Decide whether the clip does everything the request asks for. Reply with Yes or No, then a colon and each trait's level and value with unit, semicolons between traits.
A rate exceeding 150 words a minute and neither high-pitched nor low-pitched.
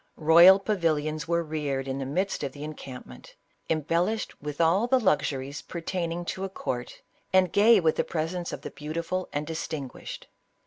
Yes: average, 175 wpm; medium, 165 Hz